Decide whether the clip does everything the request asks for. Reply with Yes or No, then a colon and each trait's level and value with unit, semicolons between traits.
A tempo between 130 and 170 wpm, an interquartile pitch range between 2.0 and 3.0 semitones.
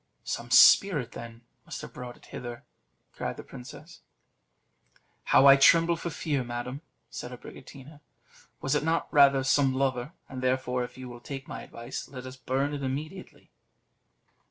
Yes: average, 155 wpm; narrow, 2.4 semitones